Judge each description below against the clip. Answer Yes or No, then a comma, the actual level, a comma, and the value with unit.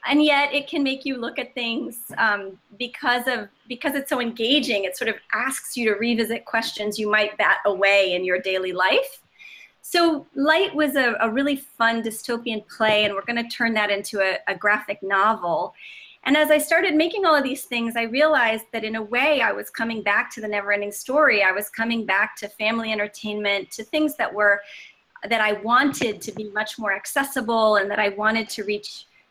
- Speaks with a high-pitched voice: Yes, high, 230 Hz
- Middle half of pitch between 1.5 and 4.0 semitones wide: No, average, 4.8 semitones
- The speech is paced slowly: No, fast, 205 wpm